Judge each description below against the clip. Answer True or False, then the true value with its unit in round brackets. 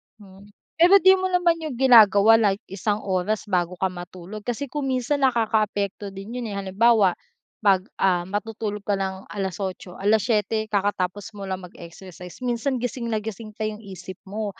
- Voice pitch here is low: False (205 Hz)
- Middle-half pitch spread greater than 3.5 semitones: False (3.1 semitones)